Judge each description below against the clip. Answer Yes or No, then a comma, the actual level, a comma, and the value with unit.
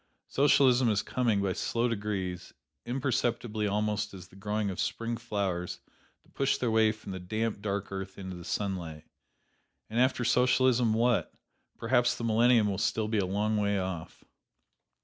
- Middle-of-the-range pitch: No, low, 105 Hz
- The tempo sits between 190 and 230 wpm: No, average, 160 wpm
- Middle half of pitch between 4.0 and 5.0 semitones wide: No, average, 3.2 semitones